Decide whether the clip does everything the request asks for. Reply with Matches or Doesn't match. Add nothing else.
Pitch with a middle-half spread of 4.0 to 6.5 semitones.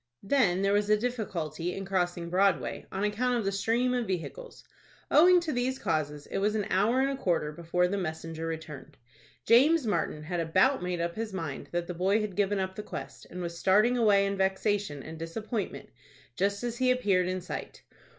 Matches